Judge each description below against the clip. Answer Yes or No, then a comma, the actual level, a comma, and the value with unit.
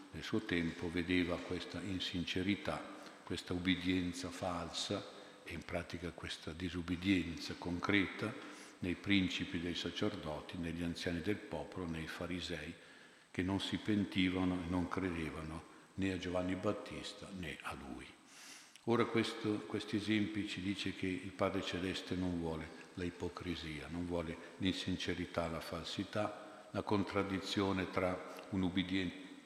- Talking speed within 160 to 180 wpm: No, average, 130 wpm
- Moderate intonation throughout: No, narrow, 2.3 semitones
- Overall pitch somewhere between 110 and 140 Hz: No, very low, 90 Hz